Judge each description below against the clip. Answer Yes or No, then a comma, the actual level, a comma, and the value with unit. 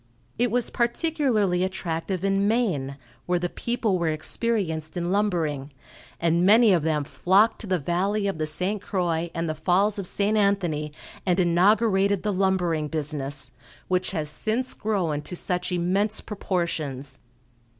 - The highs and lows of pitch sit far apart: No, average, 4.1 semitones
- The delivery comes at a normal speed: Yes, average, 150 wpm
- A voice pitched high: No, medium, 180 Hz